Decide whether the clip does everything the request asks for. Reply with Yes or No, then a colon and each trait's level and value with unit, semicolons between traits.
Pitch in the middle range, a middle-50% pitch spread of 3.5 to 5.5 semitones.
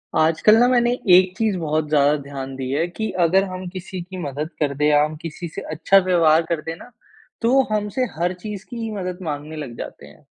Yes: medium, 170 Hz; average, 4.3 semitones